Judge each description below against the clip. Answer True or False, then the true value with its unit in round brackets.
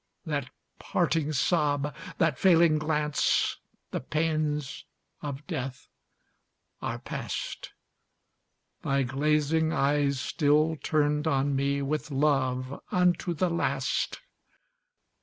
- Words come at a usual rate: False (95 wpm)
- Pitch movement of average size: False (2.2 semitones)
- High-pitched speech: False (150 Hz)